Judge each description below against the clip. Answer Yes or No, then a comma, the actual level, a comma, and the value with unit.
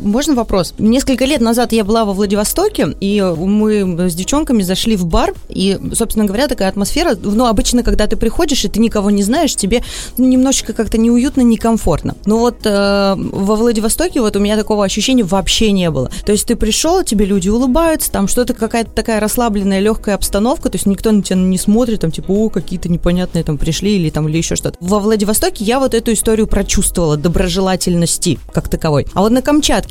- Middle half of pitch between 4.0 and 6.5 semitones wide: No, average, 3.4 semitones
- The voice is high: Yes, high, 215 Hz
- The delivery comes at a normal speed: No, fast, 195 wpm